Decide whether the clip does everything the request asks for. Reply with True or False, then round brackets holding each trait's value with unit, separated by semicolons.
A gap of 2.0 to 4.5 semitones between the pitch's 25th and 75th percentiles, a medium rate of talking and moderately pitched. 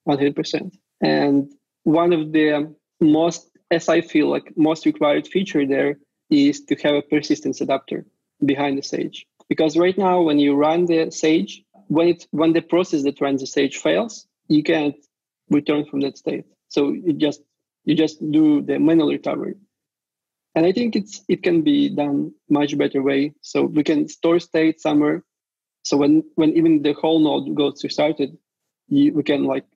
True (3.1 semitones; 175 wpm; 155 Hz)